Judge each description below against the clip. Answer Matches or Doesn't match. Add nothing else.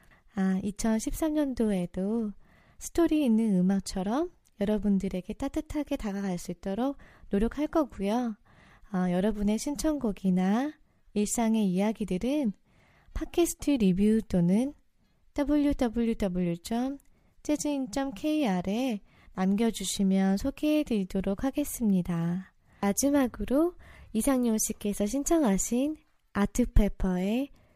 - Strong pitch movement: Matches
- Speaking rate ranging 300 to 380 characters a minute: Doesn't match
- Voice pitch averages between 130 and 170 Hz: Doesn't match